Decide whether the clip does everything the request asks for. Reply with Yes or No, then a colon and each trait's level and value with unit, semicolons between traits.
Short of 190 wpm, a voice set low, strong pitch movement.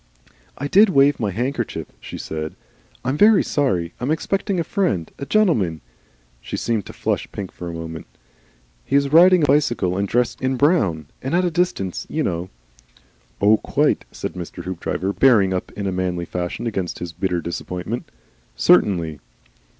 Yes: average, 175 wpm; low, 105 Hz; wide, 8.5 semitones